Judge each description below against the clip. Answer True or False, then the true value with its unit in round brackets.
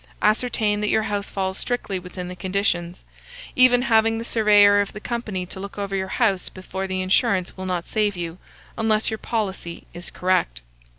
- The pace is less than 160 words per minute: False (180 wpm)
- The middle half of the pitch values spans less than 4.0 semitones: True (2.7 semitones)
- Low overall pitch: False (200 Hz)